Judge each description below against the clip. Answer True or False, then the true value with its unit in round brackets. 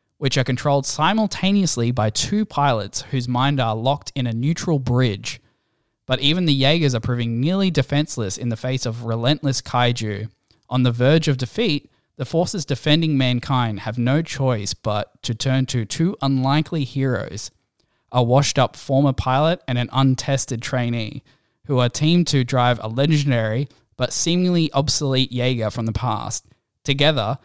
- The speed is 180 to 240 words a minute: False (155 wpm)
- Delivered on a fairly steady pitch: False (3.1 semitones)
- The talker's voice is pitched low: True (130 Hz)